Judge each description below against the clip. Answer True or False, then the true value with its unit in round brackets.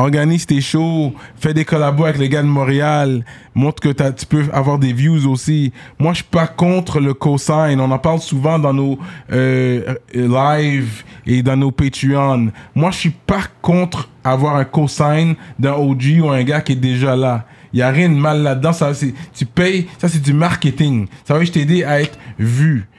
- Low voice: False (145 Hz)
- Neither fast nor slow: True (205 wpm)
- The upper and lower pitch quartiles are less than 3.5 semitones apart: True (2.9 semitones)